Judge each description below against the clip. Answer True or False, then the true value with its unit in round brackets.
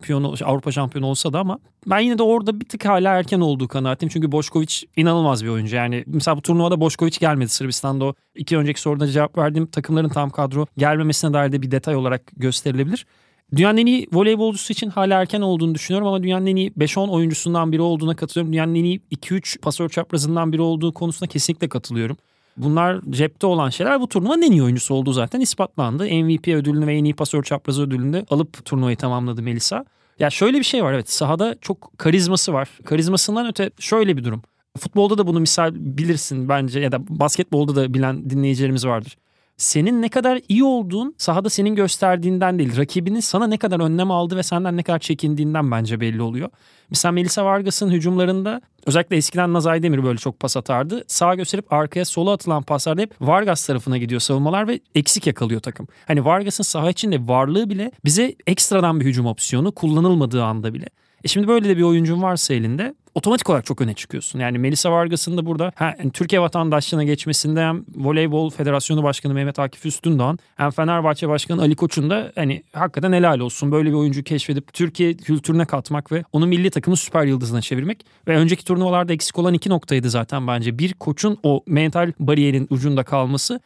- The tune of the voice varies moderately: True (4.5 semitones)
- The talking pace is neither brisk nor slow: False (185 wpm)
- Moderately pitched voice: True (160 Hz)